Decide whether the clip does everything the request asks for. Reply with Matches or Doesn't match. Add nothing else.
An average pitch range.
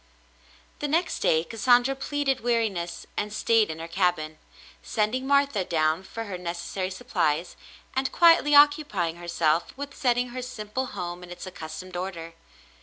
Doesn't match